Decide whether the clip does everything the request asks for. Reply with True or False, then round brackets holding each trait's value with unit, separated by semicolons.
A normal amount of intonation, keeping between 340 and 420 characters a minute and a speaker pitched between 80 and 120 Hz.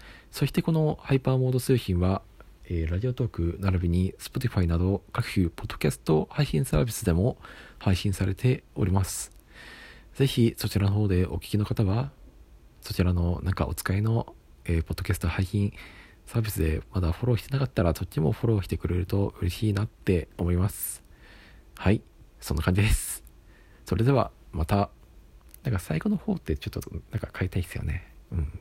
True (4.6 semitones; 380 characters per minute; 95 Hz)